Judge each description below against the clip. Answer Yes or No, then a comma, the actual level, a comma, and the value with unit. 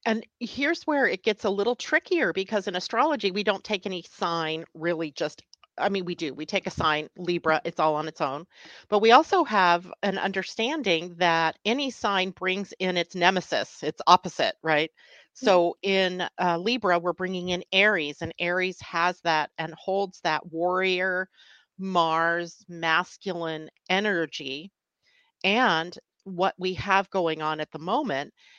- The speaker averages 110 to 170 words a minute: Yes, average, 160 wpm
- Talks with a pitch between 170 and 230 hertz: Yes, medium, 185 Hz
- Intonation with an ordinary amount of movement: Yes, average, 3.3 semitones